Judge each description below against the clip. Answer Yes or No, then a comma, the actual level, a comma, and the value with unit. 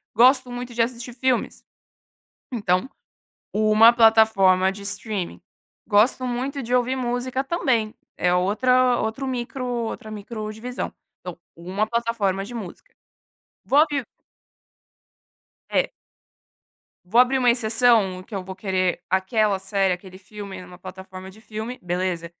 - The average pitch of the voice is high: Yes, high, 220 Hz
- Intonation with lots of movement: No, average, 4.4 semitones